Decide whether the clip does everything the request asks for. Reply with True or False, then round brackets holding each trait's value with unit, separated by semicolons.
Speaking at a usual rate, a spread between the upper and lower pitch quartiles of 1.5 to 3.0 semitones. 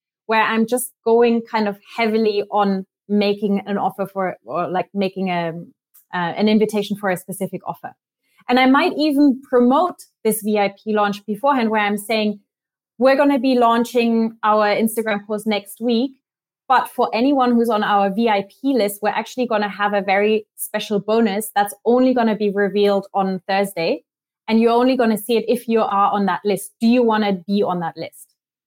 True (190 wpm; 2.5 semitones)